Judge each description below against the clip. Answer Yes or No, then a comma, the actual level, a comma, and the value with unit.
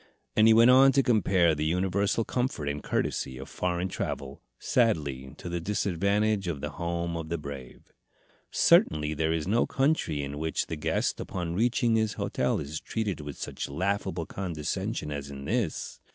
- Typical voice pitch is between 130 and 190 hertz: No, very low, 85 Hz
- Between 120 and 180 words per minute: Yes, average, 170 wpm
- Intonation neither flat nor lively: No, wide, 5.7 semitones